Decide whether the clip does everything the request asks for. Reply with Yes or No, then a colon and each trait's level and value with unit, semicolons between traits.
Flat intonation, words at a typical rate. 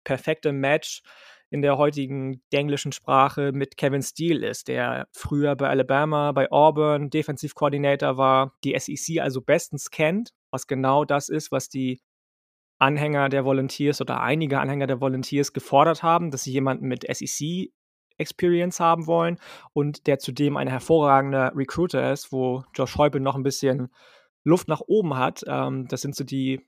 Yes: narrow, 2.0 semitones; average, 155 wpm